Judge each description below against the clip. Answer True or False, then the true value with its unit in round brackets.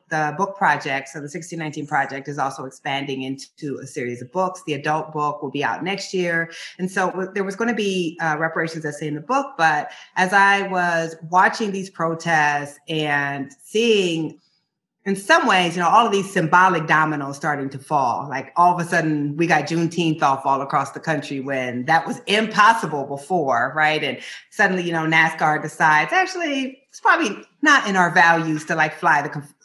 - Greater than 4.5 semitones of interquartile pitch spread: False (3.9 semitones)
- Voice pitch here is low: False (160 Hz)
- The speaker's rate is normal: True (195 wpm)